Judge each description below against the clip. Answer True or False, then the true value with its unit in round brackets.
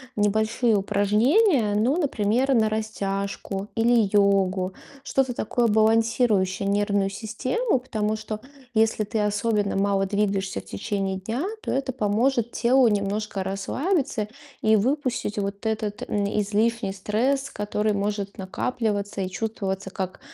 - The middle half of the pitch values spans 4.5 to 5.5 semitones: False (2.7 semitones)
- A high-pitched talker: True (210 Hz)